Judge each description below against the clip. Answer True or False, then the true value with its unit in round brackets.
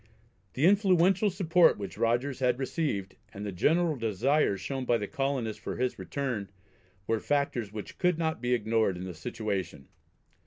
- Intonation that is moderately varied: False (6.9 semitones)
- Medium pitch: False (125 Hz)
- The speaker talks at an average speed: True (160 wpm)